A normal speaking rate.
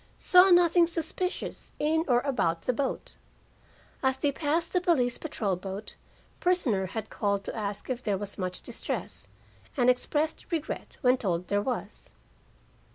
Yes: average, 150 wpm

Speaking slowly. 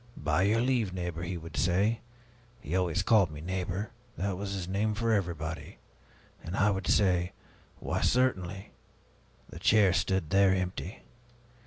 No: average, 150 wpm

